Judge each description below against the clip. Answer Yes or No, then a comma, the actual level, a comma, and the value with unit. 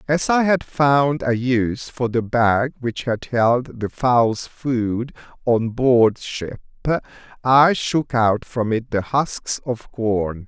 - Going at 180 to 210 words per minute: No, average, 155 wpm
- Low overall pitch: Yes, low, 120 Hz